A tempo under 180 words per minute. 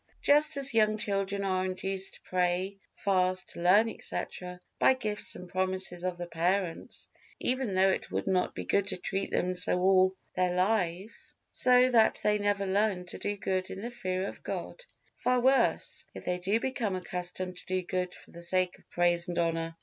No: average, 185 wpm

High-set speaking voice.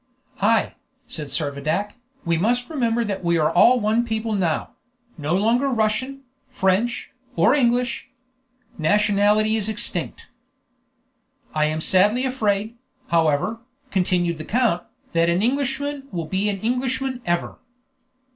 Yes: high, 210 Hz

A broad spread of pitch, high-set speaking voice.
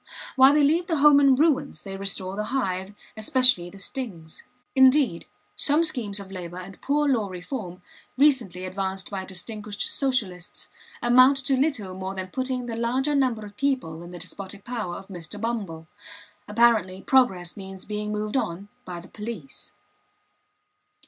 Yes: wide, 5.8 semitones; high, 210 Hz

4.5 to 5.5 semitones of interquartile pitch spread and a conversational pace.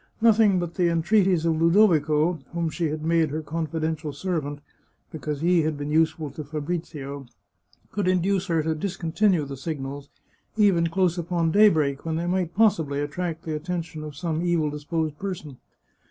No: average, 2.7 semitones; average, 170 wpm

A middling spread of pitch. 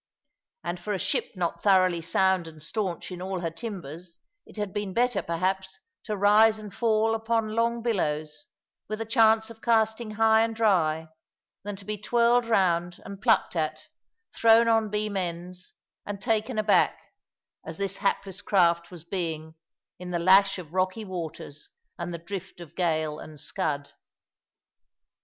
Yes: average, 4.2 semitones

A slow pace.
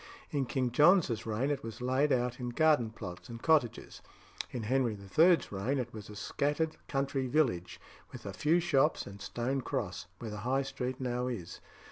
No: average, 185 wpm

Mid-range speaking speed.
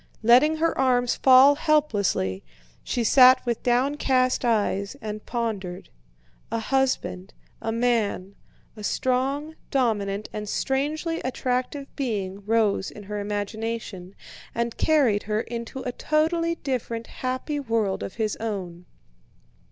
No: slow, 120 wpm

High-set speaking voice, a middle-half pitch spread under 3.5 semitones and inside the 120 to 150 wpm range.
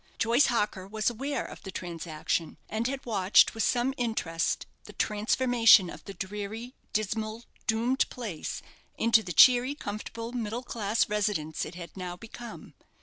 No: high, 220 Hz; average, 3.8 semitones; average, 145 wpm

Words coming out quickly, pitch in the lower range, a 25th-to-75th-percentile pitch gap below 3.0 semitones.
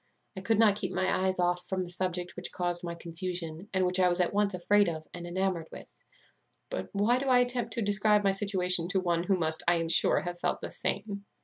No: fast, 235 wpm; medium, 185 Hz; narrow, 2.6 semitones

